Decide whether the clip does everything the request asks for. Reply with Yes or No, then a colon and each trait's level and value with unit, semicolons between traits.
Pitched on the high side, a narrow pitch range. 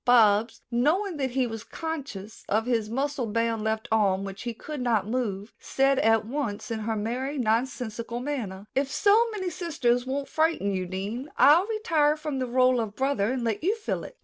No: high, 245 Hz; average, 4.7 semitones